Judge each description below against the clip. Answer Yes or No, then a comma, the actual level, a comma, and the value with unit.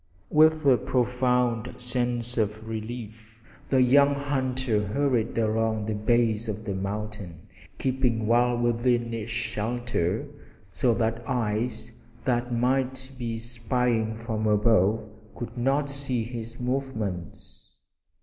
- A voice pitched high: No, low, 120 Hz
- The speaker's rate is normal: No, slow, 115 wpm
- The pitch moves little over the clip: Yes, narrow, 2.2 semitones